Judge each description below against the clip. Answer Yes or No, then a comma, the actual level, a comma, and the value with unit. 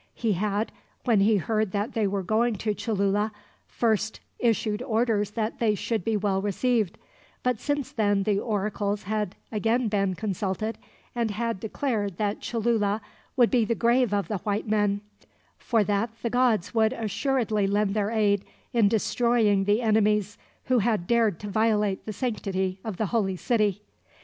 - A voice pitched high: Yes, high, 215 Hz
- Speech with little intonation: Yes, narrow, 2.2 semitones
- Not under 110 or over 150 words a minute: No, average, 165 wpm